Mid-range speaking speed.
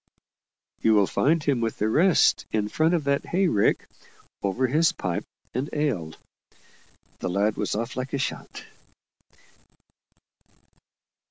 No: slow, 125 wpm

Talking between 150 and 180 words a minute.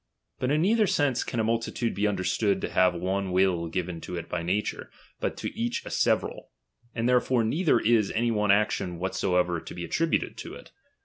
No: average, 195 wpm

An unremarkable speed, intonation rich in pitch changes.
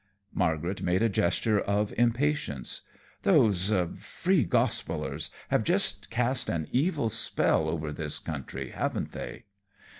No: slow, 120 wpm; wide, 7.1 semitones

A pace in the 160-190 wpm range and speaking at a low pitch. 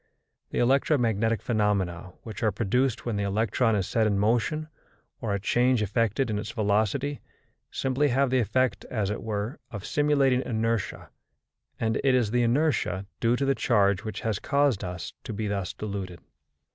Yes: average, 170 wpm; low, 110 Hz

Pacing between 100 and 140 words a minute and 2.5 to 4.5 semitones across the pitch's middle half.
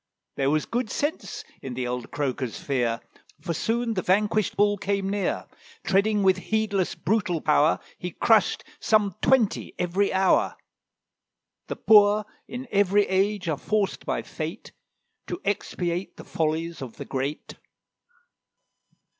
No: slow, 135 wpm; average, 4.9 semitones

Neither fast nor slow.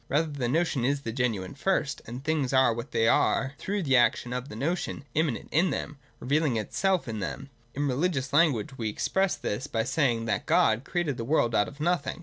No: fast, 215 wpm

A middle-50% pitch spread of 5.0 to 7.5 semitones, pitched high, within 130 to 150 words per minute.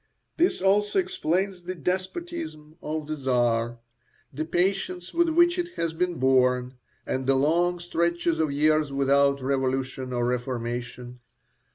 No: wide, 5.6 semitones; medium, 155 Hz; slow, 135 wpm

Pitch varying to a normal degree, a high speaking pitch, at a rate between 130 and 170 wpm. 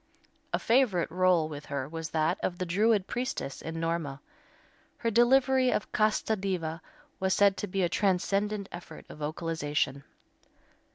No: average, 4.6 semitones; medium, 180 Hz; average, 150 wpm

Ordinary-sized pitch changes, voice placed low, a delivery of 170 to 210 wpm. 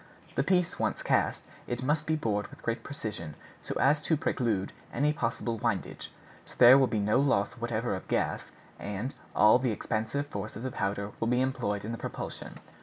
Yes: average, 4.5 semitones; low, 120 Hz; average, 190 wpm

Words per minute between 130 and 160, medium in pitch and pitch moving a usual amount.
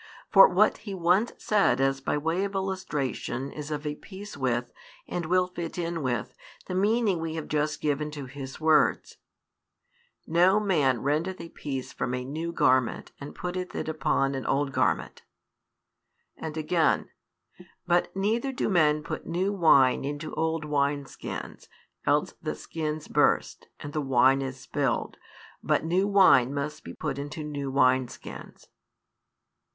Yes: average, 155 wpm; medium, 150 Hz; average, 4.4 semitones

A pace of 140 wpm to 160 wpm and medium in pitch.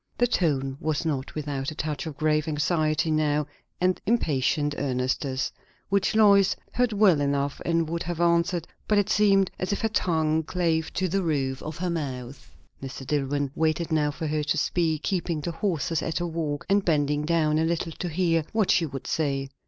No: average, 190 wpm; medium, 160 Hz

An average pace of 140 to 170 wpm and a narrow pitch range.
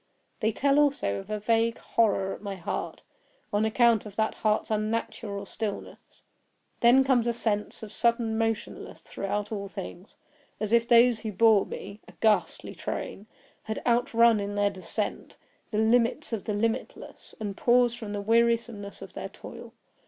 Yes: average, 160 wpm; narrow, 2.2 semitones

